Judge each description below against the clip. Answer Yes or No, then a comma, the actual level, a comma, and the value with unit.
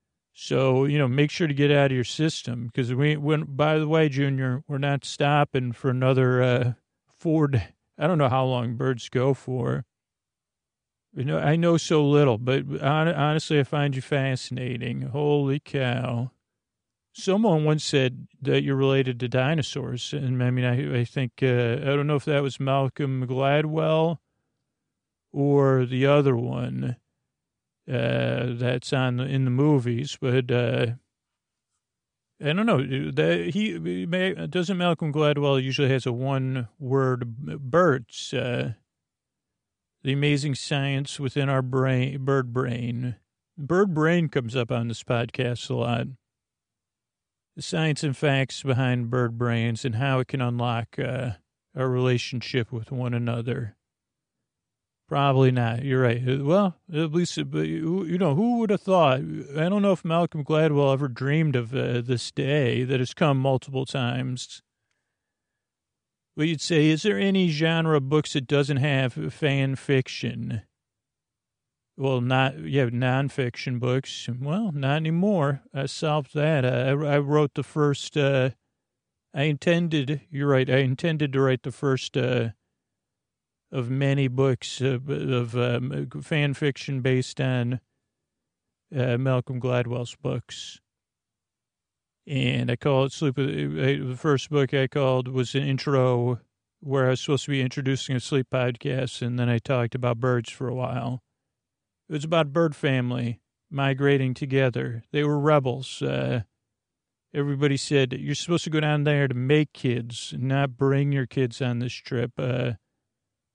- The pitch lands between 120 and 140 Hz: Yes, low, 135 Hz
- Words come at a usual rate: Yes, average, 150 wpm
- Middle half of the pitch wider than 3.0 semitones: No, average, 2.7 semitones